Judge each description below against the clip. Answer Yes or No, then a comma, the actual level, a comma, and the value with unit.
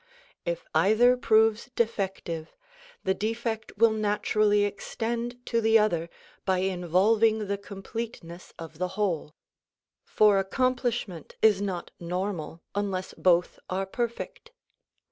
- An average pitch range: Yes, average, 3.4 semitones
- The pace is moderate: No, slow, 110 wpm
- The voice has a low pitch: No, high, 205 Hz